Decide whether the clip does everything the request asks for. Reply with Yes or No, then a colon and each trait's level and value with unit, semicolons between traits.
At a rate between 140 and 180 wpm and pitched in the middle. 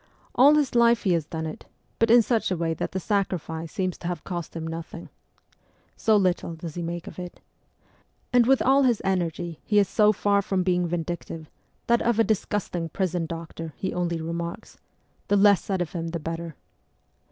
No: average, 195 wpm; medium, 180 Hz